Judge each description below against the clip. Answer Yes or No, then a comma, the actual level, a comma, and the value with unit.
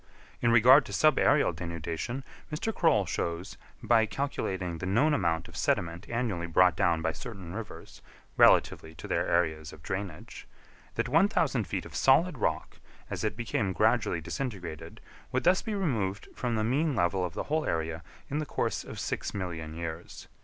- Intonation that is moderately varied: No, wide, 7.7 semitones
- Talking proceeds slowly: No, average, 165 wpm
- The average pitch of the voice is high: No, very low, 95 Hz